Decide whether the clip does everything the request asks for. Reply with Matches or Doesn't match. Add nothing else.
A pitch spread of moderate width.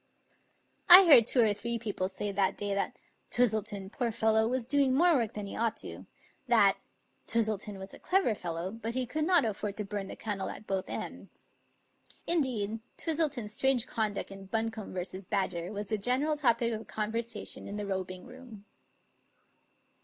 Matches